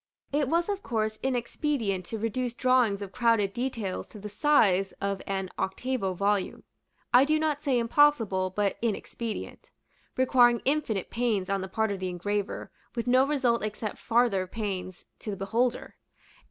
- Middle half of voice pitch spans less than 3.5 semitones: No, average, 4.4 semitones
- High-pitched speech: Yes, high, 225 Hz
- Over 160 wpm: No, average, 155 wpm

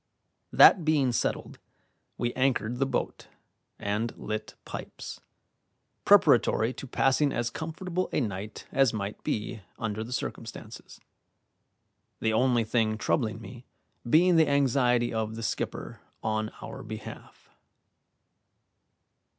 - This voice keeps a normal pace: No, slow, 115 wpm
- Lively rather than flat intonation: No, average, 3.8 semitones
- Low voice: Yes, low, 120 Hz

